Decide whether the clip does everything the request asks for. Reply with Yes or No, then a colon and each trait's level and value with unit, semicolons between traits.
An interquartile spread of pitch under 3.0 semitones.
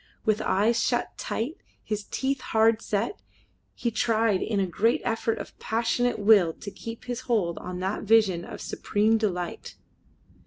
Yes: narrow, 2.5 semitones